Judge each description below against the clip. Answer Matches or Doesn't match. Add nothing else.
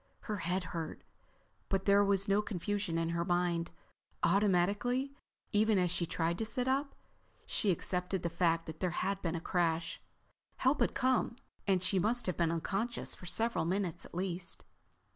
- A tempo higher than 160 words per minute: Matches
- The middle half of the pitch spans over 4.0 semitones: Doesn't match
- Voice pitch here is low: Doesn't match